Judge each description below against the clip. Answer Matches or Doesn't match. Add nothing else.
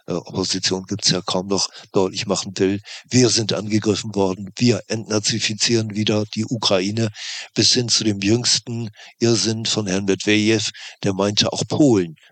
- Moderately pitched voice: Doesn't match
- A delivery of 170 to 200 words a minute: Doesn't match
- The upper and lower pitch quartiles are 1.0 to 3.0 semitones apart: Matches